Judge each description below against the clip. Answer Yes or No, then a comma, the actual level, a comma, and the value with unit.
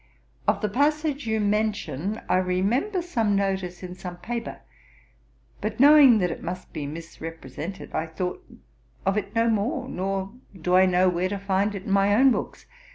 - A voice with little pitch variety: No, average, 3.9 semitones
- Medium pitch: No, high, 195 Hz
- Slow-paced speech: No, average, 170 wpm